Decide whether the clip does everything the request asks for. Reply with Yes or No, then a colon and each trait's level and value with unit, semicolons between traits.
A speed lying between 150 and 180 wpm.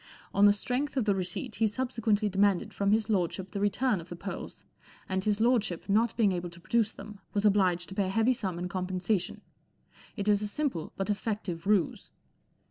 No: average, 200 wpm